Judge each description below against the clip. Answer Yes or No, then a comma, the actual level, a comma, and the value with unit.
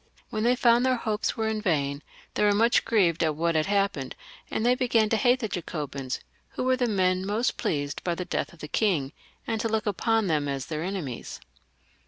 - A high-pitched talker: Yes, high, 200 Hz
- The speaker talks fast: Yes, fast, 210 wpm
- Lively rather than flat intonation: Yes, wide, 6.3 semitones